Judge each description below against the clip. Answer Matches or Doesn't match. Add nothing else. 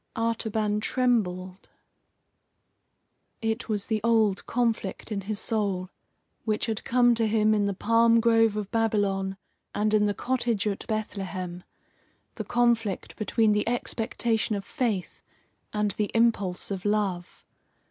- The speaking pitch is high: Matches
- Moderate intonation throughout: Doesn't match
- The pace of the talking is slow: Matches